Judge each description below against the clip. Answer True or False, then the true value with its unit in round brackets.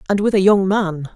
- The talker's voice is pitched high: True (195 Hz)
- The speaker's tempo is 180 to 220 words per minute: False (260 wpm)